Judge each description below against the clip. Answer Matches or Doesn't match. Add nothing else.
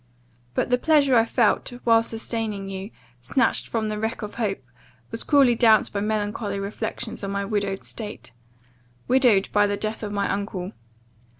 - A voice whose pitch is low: Doesn't match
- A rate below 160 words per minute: Doesn't match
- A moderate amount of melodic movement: Doesn't match